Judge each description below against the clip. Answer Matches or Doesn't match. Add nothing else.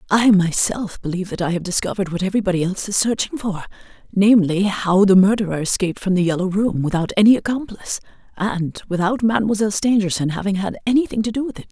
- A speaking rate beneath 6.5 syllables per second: Doesn't match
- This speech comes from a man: Doesn't match